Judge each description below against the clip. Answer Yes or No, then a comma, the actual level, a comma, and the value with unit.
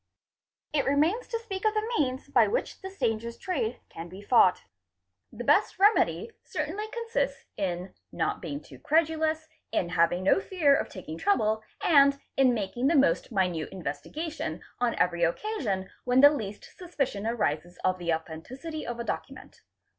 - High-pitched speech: Yes, very high, 250 Hz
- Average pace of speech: Yes, average, 160 wpm